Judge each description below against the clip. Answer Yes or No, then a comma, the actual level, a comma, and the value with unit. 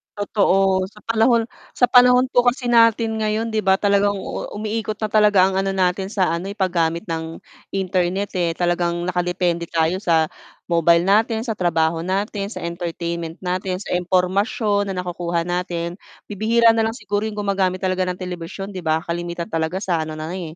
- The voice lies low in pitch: No, medium, 185 Hz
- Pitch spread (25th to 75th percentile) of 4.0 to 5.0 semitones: No, average, 3.4 semitones